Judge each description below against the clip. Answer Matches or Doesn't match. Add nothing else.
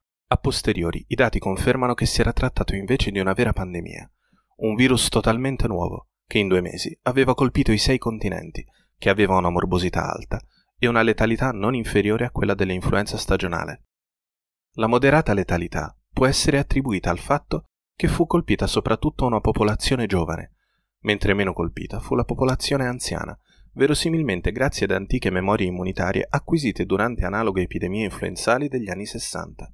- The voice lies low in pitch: Matches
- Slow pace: Doesn't match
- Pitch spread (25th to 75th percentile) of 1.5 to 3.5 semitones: Doesn't match